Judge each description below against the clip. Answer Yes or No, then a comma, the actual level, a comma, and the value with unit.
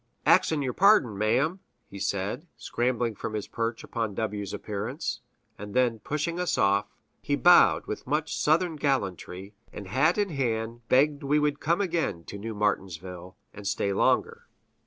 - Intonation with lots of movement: Yes, wide, 6.6 semitones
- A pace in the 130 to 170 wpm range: Yes, average, 160 wpm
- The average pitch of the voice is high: No, low, 115 Hz